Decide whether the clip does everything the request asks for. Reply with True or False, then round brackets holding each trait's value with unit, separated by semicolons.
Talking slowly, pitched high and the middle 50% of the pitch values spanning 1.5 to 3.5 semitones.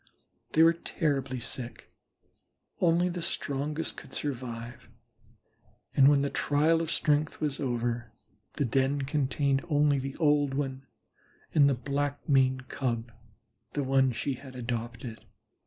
False (130 wpm; 135 Hz; 2.4 semitones)